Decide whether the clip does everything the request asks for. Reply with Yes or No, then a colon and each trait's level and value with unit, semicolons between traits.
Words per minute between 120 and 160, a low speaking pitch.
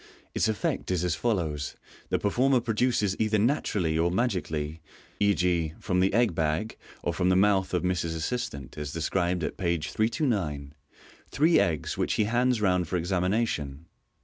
Yes: average, 155 wpm; very low, 90 Hz